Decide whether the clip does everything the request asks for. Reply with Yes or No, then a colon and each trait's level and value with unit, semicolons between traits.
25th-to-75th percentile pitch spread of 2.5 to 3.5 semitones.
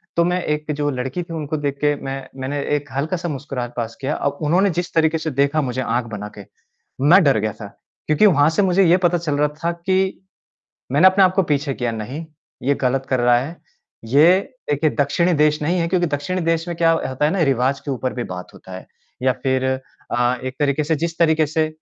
No: average, 4.1 semitones